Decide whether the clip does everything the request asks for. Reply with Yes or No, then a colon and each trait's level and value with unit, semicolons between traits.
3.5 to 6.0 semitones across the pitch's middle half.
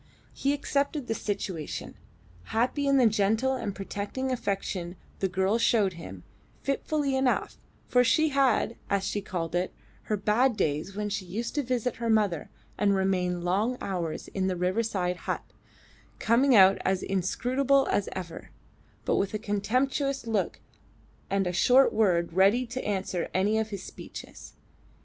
Yes: average, 4.8 semitones